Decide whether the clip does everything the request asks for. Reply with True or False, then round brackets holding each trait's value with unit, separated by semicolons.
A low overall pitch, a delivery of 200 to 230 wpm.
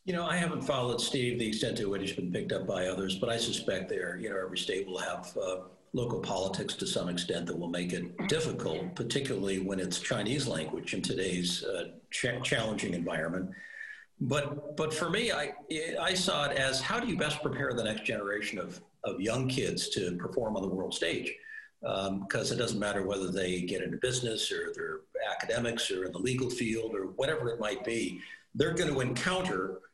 True (125 Hz; 205 wpm)